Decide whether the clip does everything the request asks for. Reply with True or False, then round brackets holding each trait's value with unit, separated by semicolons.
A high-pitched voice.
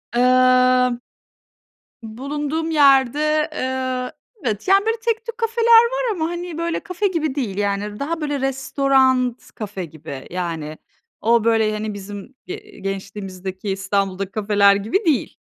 True (255 Hz)